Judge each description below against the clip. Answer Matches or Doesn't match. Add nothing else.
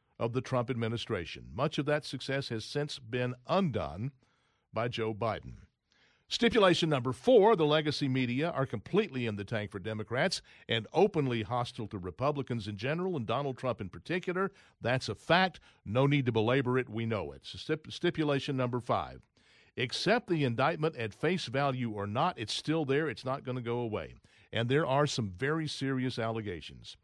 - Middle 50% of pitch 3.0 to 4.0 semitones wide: Doesn't match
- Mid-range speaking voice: Doesn't match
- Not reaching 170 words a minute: Doesn't match